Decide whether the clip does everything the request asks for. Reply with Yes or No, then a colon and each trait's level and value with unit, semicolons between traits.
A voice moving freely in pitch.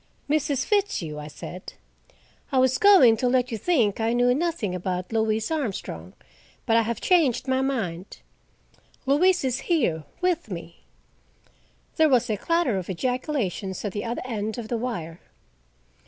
Yes: wide, 6.0 semitones